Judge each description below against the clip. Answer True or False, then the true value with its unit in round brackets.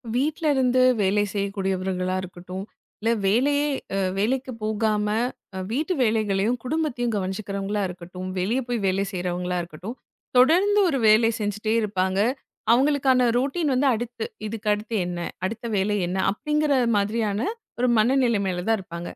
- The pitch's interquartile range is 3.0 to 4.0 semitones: False (4.7 semitones)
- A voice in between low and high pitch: False (215 Hz)